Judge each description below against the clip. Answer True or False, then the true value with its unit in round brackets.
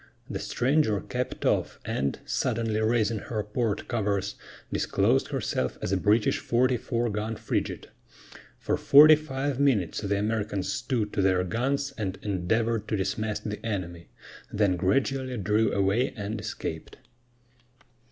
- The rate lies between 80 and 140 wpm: True (135 wpm)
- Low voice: True (110 Hz)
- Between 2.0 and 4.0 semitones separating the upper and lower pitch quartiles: True (3.3 semitones)